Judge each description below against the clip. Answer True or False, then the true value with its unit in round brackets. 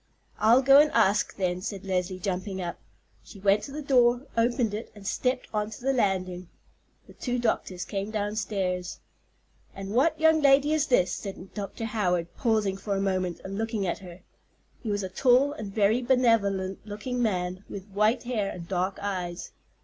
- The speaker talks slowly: False (180 wpm)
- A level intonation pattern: False (4.2 semitones)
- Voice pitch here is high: True (205 Hz)